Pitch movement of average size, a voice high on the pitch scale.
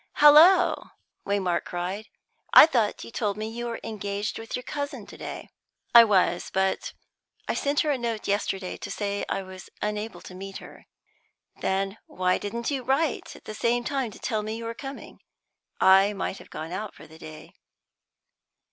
Yes: average, 3.8 semitones; high, 215 Hz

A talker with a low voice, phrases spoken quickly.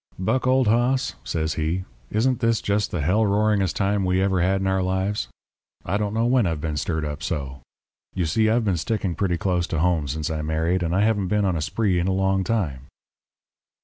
Yes: very low, 95 Hz; fast, 215 wpm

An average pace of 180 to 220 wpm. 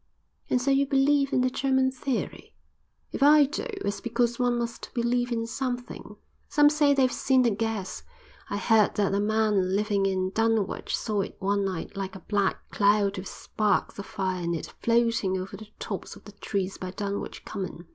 Yes: average, 185 wpm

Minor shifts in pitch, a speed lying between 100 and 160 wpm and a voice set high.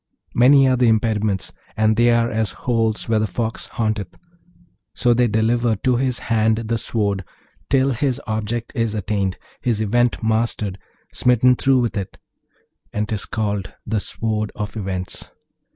No: narrow, 2.1 semitones; average, 150 wpm; low, 110 Hz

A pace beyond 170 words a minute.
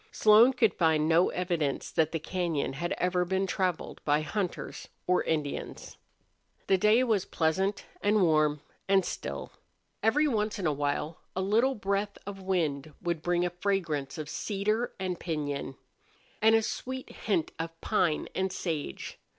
No: average, 155 wpm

